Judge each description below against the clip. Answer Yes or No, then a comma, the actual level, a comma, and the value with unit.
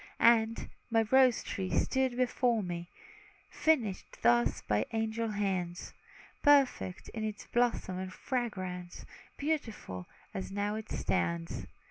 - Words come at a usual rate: No, slow, 115 wpm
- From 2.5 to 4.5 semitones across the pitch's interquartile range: No, average, 5.1 semitones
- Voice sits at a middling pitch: No, high, 210 Hz